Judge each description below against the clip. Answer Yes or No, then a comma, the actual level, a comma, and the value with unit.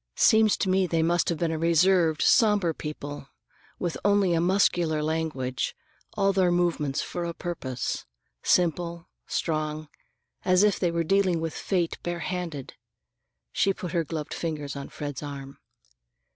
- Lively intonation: No, average, 2.9 semitones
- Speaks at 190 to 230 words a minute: No, average, 150 wpm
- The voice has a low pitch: No, medium, 170 Hz